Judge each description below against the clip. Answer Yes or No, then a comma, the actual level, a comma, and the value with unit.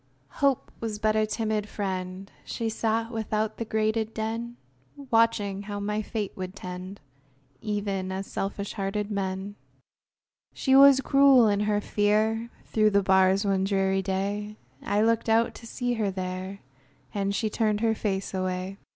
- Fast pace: No, average, 150 wpm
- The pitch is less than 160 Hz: No, high, 210 Hz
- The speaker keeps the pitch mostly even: Yes, narrow, 2.3 semitones